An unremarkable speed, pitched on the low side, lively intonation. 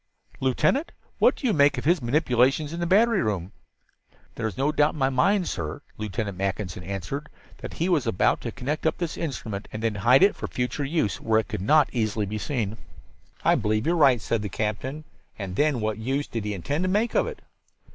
No: fast, 215 wpm; low, 125 Hz; wide, 6.4 semitones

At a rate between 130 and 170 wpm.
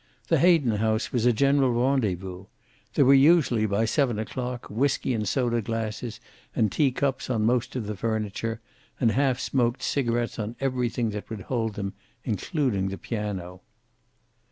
Yes: average, 155 wpm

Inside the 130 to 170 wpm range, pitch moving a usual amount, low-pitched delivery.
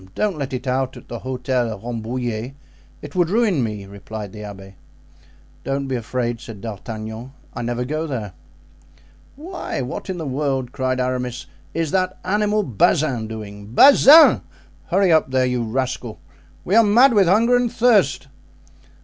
No: average, 155 wpm; wide, 7.3 semitones; low, 130 Hz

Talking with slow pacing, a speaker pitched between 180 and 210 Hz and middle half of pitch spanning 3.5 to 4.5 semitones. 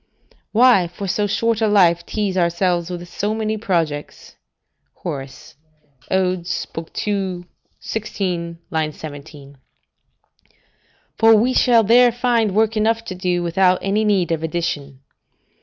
Yes: slow, 120 wpm; medium, 185 Hz; average, 4.1 semitones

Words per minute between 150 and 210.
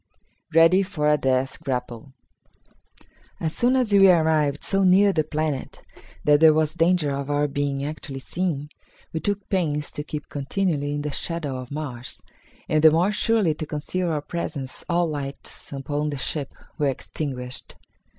Yes: average, 160 wpm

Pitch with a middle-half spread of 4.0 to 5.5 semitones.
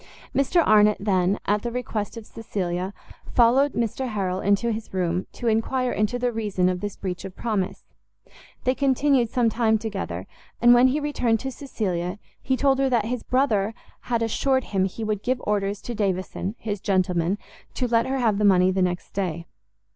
Yes: average, 4.3 semitones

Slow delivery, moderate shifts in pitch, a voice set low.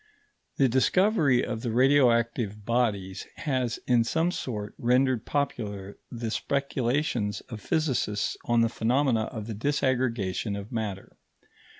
Yes: slow, 120 wpm; average, 3.5 semitones; low, 120 Hz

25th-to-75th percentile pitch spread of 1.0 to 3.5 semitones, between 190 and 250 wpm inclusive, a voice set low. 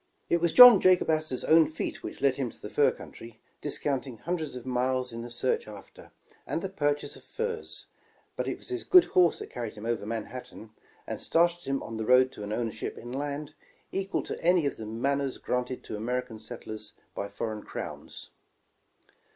No: wide, 5.6 semitones; average, 195 wpm; low, 130 Hz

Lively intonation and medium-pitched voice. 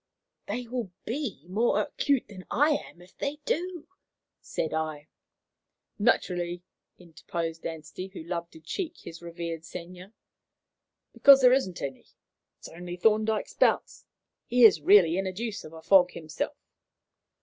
Yes: wide, 5.7 semitones; medium, 180 Hz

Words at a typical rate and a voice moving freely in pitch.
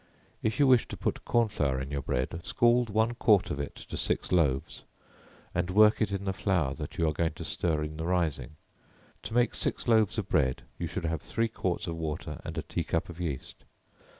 No: fast, 220 wpm; wide, 6.0 semitones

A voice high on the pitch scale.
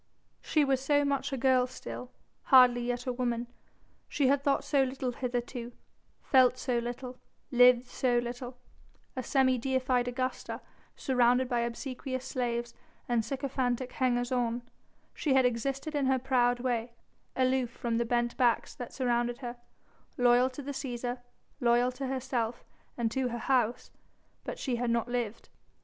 Yes: very high, 250 Hz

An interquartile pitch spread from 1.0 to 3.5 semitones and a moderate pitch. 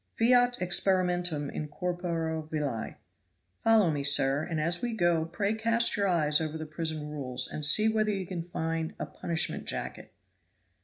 No: average, 4.3 semitones; medium, 170 Hz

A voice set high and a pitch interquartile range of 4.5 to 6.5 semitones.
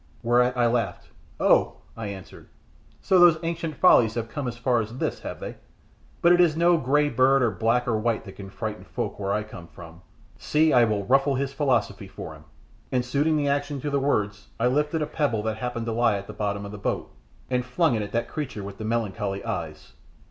No: low, 120 Hz; average, 5.3 semitones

